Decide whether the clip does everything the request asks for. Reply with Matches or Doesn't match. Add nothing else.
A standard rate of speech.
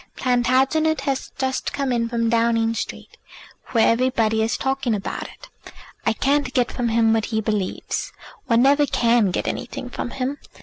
Matches